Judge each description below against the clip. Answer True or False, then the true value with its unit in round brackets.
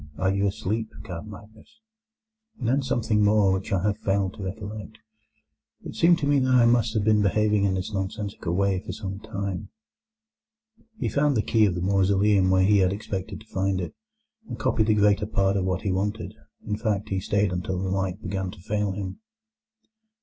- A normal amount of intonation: False (2.3 semitones)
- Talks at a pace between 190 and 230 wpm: True (195 wpm)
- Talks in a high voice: False (100 Hz)